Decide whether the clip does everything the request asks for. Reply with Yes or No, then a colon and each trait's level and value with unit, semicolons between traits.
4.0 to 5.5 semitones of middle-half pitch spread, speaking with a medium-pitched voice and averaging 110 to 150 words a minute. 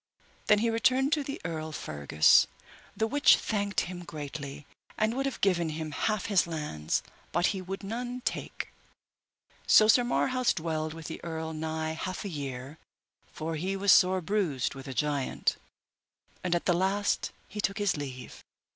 No: average, 5.2 semitones; medium, 175 Hz; average, 165 wpm